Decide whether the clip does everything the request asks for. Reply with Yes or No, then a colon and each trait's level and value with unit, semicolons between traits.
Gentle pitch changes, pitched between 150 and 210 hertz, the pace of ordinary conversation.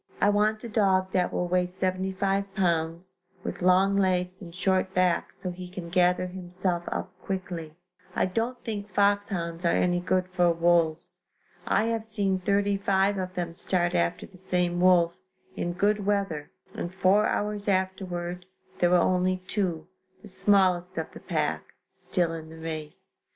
Yes: narrow, 2.0 semitones; medium, 185 Hz; average, 160 wpm